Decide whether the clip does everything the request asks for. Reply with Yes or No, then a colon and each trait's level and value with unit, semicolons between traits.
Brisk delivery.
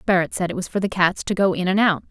Yes: fast, 340 wpm